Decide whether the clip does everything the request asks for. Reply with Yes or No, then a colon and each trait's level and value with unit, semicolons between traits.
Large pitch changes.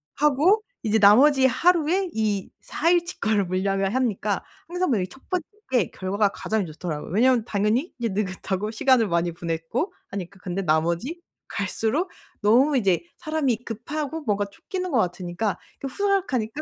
Yes: wide, 7.1 semitones